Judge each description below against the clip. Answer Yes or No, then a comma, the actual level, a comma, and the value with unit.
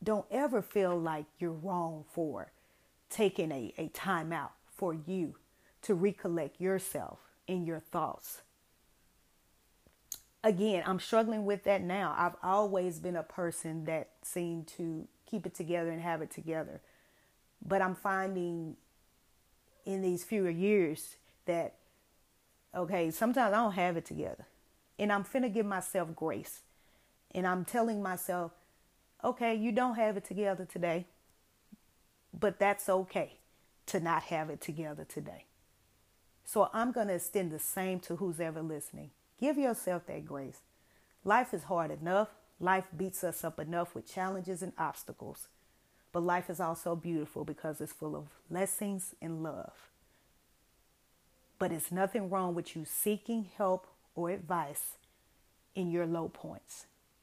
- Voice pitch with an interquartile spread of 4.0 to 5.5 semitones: No, average, 3.1 semitones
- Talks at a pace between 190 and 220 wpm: No, average, 145 wpm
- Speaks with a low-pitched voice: No, medium, 180 Hz